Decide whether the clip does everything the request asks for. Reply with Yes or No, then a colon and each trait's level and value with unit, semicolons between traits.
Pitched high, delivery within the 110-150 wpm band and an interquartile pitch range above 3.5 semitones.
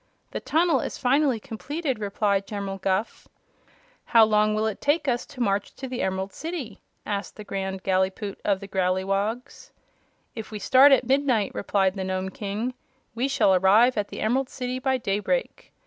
No: high, 215 Hz; average, 170 wpm; average, 4.7 semitones